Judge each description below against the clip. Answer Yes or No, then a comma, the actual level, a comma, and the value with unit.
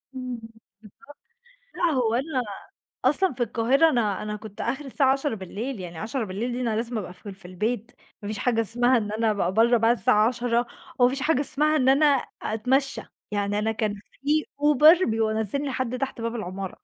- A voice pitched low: No, high, 235 Hz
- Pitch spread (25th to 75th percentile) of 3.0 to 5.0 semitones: Yes, average, 3.8 semitones